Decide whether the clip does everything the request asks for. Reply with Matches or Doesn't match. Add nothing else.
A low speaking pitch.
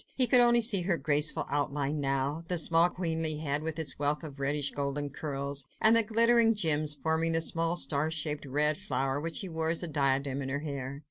Doesn't match